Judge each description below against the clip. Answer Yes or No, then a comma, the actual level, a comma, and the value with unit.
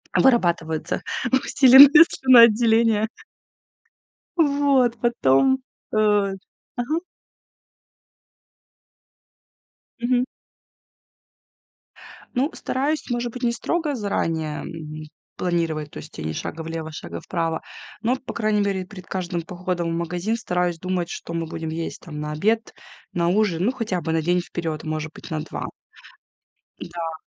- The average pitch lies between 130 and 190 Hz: Yes, medium, 185 Hz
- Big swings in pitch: Yes, wide, 6.5 semitones